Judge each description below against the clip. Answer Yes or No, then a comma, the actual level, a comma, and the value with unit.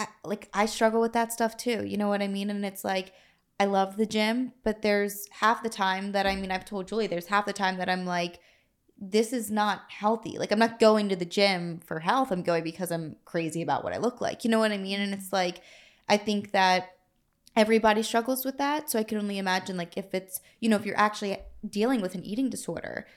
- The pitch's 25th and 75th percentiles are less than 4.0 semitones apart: Yes, average, 2.7 semitones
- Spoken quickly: Yes, fast, 245 wpm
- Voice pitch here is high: Yes, high, 205 Hz